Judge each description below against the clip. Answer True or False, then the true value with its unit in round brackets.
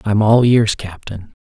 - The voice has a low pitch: True (105 Hz)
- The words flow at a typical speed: True (165 wpm)